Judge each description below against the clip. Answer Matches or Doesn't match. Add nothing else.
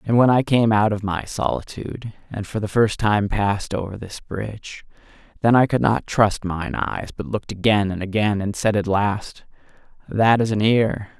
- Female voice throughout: Doesn't match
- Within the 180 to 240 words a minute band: Matches